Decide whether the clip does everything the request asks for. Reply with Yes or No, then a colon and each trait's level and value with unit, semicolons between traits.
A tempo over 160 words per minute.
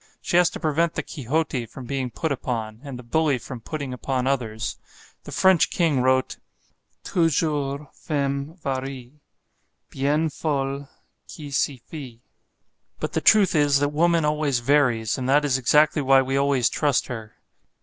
No: average, 155 wpm